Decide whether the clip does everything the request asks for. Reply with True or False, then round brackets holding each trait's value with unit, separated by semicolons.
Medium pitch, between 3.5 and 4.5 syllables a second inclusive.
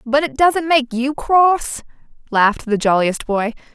False (260 Hz; 4.0 syllables/s)